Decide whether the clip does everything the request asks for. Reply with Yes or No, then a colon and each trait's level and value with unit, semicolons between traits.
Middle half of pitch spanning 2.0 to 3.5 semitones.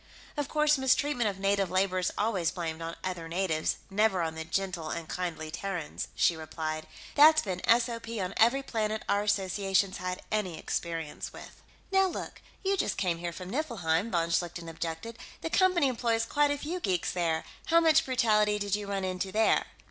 No: average, 5.3 semitones